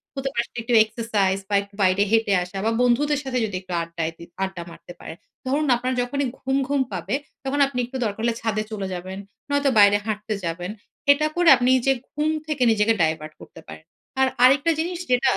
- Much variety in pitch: Yes, wide, 5.8 semitones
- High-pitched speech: Yes, high, 225 Hz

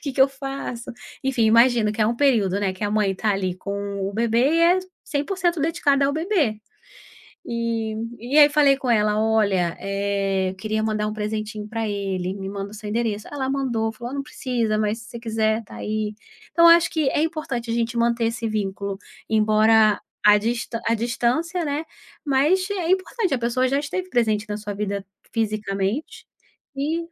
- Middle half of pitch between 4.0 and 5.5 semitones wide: Yes, average, 4.6 semitones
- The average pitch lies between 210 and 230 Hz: Yes, high, 225 Hz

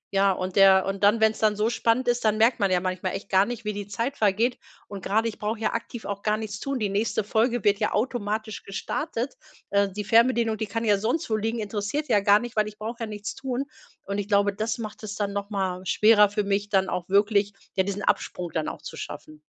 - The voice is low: No, high, 210 Hz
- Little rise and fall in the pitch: Yes, narrow, 2.2 semitones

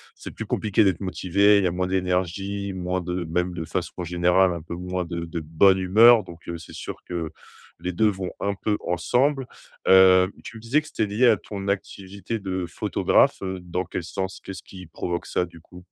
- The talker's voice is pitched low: Yes, very low, 95 Hz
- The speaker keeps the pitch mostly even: Yes, narrow, 2.1 semitones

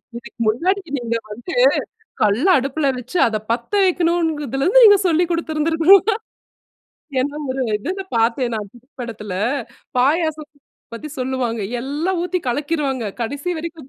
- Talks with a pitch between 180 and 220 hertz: No, very high, 285 Hz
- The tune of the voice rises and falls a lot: Yes, wide, 5.8 semitones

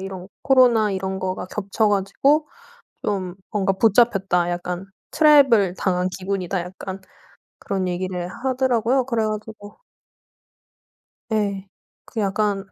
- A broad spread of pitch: No, average, 3.1 semitones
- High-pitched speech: Yes, high, 195 Hz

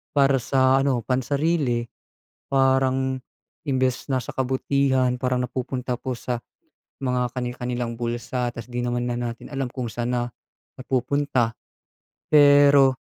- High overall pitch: No, low, 130 Hz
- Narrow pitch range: Yes, narrow, 1.7 semitones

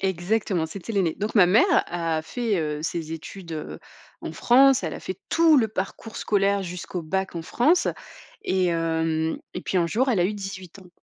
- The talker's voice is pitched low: No, medium, 185 Hz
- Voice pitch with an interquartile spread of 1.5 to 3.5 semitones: No, average, 4.3 semitones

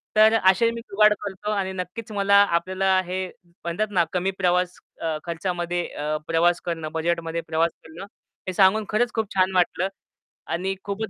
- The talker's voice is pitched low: No, medium, 185 Hz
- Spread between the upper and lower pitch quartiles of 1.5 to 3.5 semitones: Yes, average, 2.7 semitones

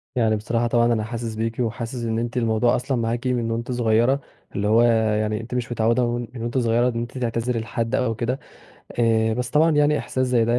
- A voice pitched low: Yes, low, 115 Hz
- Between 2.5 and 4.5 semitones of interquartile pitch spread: No, narrow, 1.5 semitones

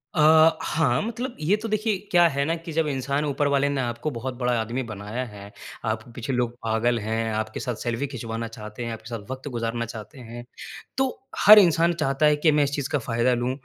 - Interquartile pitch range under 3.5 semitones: No, average, 4.9 semitones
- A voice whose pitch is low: Yes, low, 130 Hz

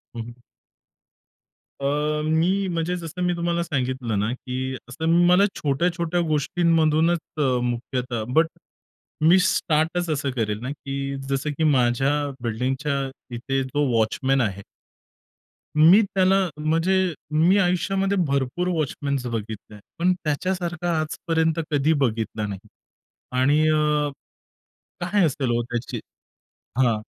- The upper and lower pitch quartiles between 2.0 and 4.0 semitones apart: No, average, 5.1 semitones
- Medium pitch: Yes, medium, 150 Hz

